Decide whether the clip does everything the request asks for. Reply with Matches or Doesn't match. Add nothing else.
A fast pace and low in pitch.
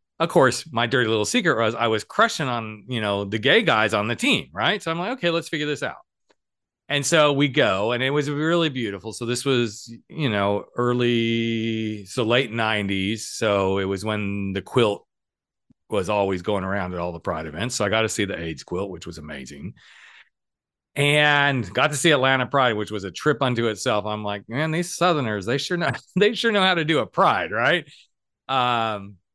Matches